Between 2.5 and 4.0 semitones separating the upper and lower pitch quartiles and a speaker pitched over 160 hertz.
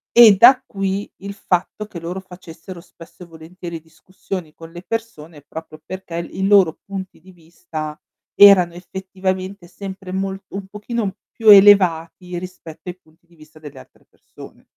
Yes: average, 2.8 semitones; medium, 185 Hz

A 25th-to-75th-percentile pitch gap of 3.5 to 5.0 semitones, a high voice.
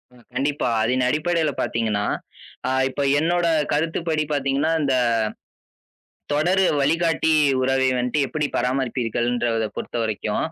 No: average, 4.4 semitones; low, 135 Hz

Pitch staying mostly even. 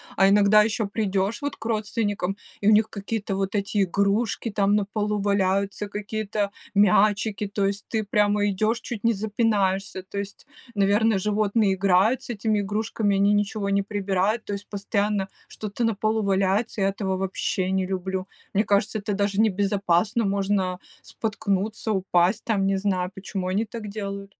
Yes: narrow, 1.6 semitones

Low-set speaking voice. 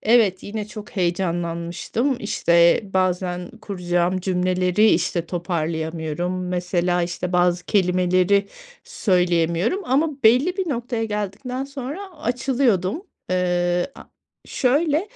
No: medium, 185 Hz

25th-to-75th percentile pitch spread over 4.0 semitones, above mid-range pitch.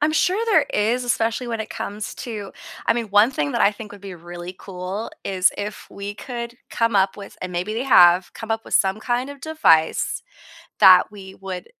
No: average, 3.7 semitones; high, 210 Hz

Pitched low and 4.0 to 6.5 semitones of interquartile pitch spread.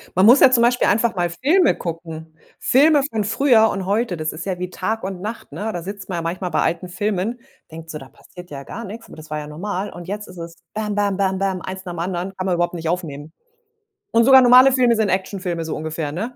No: high, 190 Hz; average, 4.5 semitones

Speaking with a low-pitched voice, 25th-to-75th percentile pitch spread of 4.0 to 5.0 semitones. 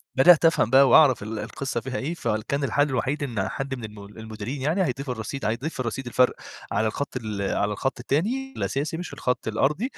Yes: low, 130 Hz; average, 4.5 semitones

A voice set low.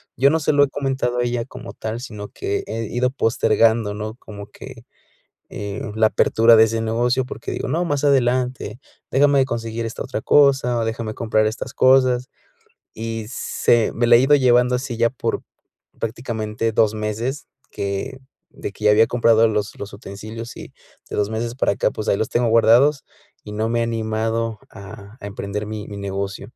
Yes: low, 115 Hz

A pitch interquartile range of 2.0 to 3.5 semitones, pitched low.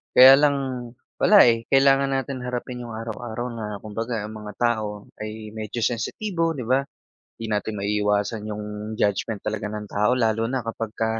Yes: average, 2.9 semitones; low, 115 Hz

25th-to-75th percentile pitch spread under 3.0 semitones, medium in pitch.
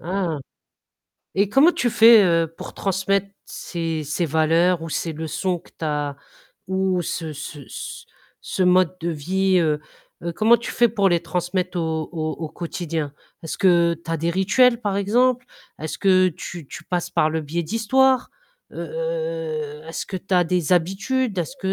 No: average, 3.7 semitones; medium, 180 Hz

